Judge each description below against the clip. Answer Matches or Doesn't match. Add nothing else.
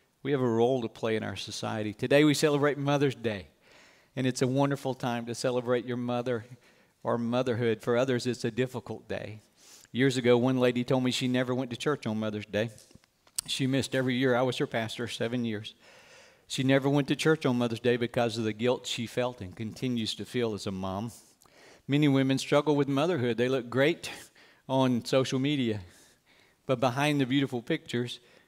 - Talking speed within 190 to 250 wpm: Matches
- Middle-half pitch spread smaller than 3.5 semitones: Matches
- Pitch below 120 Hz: Doesn't match